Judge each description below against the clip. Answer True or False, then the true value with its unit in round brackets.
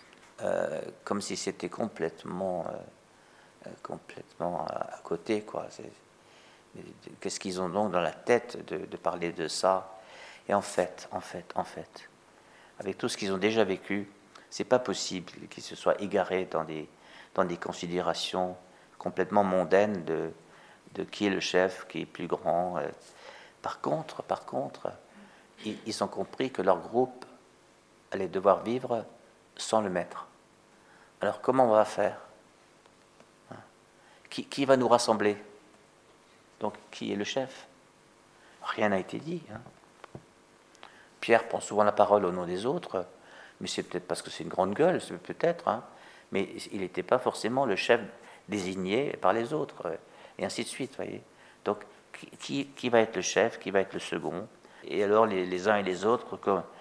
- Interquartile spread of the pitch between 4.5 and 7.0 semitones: False (3.8 semitones)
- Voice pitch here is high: False (100 Hz)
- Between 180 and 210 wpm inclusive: False (165 wpm)